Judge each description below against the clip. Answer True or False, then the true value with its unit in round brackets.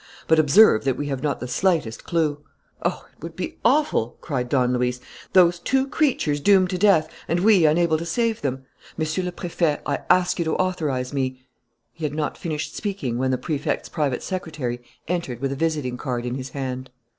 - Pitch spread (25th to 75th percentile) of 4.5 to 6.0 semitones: True (5.3 semitones)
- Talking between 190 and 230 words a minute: True (200 wpm)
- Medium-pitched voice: True (155 Hz)